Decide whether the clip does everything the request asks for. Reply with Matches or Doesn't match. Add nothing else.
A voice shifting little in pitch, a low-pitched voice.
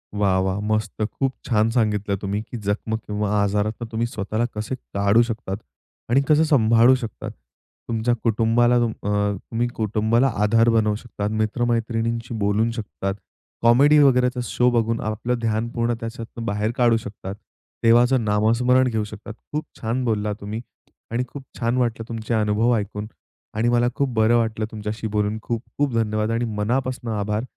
Matches